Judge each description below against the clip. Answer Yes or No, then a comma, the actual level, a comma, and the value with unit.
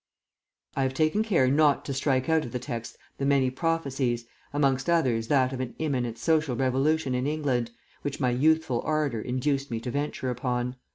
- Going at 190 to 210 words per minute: No, average, 180 wpm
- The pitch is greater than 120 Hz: Yes, low, 135 Hz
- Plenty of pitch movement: No, average, 3.1 semitones